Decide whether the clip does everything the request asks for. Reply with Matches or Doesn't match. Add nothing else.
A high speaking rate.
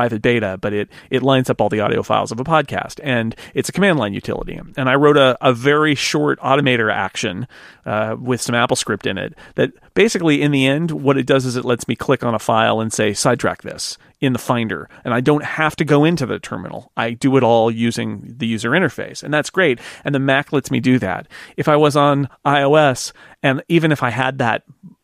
Matches